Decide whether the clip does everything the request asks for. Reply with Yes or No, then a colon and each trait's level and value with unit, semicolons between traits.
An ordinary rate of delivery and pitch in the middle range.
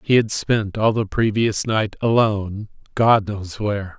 No: average, 165 wpm; low, 105 Hz